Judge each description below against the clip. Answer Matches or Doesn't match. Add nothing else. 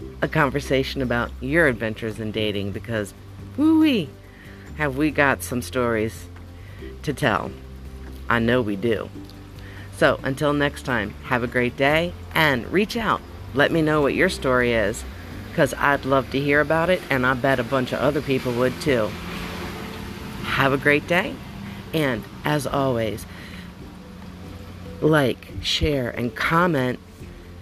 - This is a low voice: Matches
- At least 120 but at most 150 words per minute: Matches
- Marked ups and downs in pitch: Matches